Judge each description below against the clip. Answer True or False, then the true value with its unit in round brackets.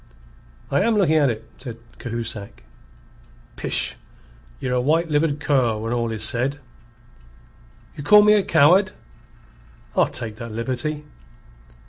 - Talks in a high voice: False (135 Hz)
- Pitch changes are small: False (5.2 semitones)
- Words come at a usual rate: False (130 wpm)